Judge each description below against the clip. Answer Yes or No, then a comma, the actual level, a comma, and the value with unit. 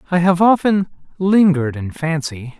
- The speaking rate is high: No, average, 140 wpm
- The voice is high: No, medium, 170 Hz